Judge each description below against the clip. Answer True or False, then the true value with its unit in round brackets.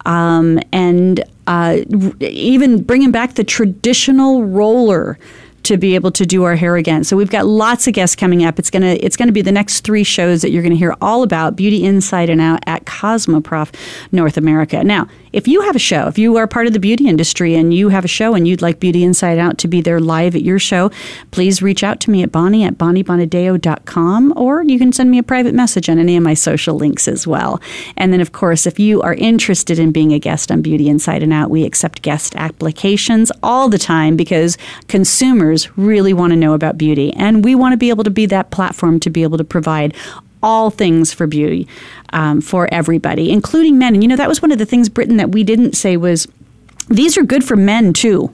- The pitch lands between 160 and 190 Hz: True (185 Hz)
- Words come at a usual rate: False (225 wpm)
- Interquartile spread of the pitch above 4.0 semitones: True (5.0 semitones)